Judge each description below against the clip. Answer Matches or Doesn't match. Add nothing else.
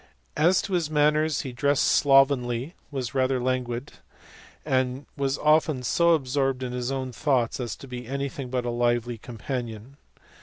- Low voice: Matches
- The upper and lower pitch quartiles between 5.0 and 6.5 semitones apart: Doesn't match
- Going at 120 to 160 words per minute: Matches